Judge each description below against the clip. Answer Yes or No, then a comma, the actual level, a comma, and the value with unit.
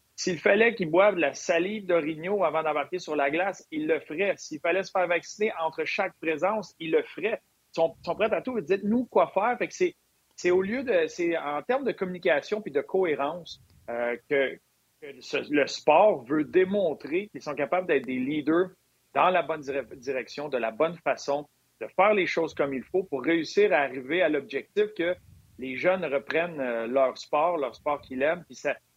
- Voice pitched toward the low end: No, medium, 170 Hz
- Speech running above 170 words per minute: Yes, average, 210 wpm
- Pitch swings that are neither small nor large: No, wide, 6.1 semitones